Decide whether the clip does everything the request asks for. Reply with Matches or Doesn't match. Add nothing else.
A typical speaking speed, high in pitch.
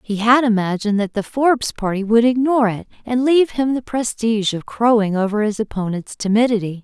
Matches